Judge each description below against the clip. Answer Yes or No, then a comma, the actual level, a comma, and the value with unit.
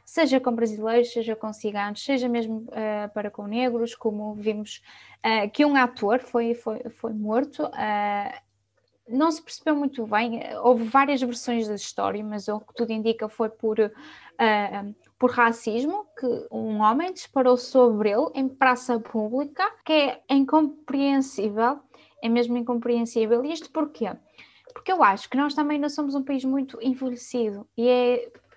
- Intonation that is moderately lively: Yes, average, 3.8 semitones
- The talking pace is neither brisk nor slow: Yes, average, 160 wpm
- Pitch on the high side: Yes, high, 240 Hz